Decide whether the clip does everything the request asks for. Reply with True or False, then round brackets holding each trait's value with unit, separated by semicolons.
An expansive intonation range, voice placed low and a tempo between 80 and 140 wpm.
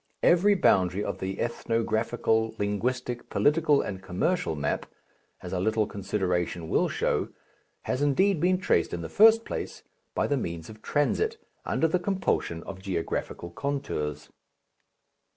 True (8.4 semitones; 110 Hz; 135 wpm)